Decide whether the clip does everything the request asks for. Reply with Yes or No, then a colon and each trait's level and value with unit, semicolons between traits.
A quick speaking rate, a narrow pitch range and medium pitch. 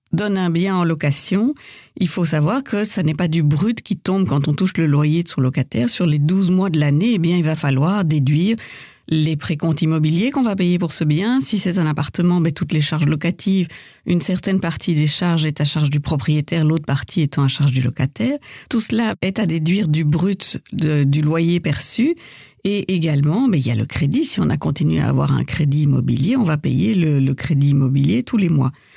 No: fast, 225 wpm; average, 4.3 semitones; medium, 165 Hz